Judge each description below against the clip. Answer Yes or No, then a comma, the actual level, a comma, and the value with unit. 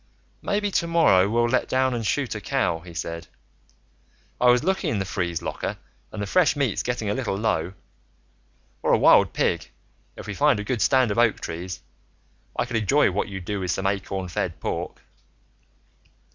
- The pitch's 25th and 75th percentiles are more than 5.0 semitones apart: Yes, wide, 5.4 semitones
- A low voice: Yes, low, 105 Hz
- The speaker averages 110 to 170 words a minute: No, average, 185 wpm